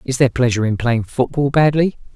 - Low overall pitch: Yes, low, 130 Hz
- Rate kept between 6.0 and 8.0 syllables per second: Yes, 6.3 syllables/s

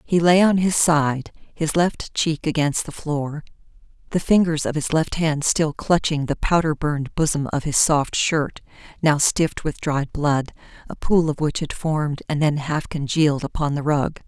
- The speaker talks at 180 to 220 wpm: Yes, average, 190 wpm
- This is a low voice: No, medium, 155 Hz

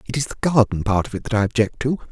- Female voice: No, male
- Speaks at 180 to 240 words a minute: No, fast, 310 wpm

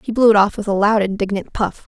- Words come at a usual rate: No, fast, 280 wpm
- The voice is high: Yes, high, 205 Hz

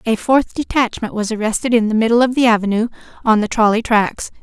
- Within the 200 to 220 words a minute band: Yes, fast, 205 wpm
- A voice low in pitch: No, high, 225 Hz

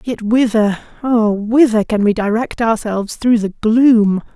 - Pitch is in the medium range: No, high, 220 Hz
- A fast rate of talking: No, average, 140 wpm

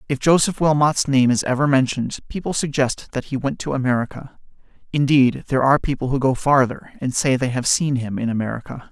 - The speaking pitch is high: No, low, 135 Hz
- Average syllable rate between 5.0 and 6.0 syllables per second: Yes, 5.9 syllables/s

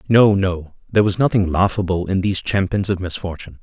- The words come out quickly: No, average, 180 wpm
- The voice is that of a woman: No, male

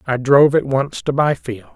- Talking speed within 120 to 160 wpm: No, fast, 205 wpm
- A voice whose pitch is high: No, low, 135 Hz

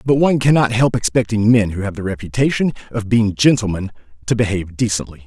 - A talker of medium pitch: No, low, 110 Hz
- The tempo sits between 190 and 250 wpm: No, average, 180 wpm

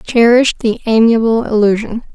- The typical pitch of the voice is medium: No, high, 225 Hz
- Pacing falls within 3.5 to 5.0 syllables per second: No, 5.5 syllables/s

